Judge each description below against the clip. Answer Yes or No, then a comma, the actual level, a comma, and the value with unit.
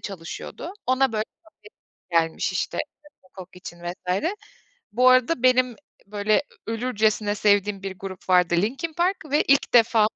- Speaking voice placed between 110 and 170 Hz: No, high, 215 Hz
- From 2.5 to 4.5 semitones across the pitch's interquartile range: No, average, 5.3 semitones